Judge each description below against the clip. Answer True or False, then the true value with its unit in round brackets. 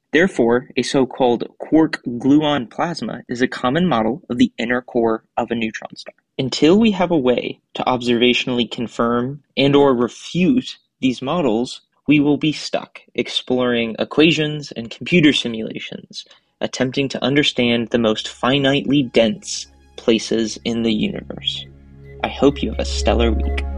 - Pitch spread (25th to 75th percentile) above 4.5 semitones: False (3.9 semitones)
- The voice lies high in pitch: False (125 Hz)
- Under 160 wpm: True (145 wpm)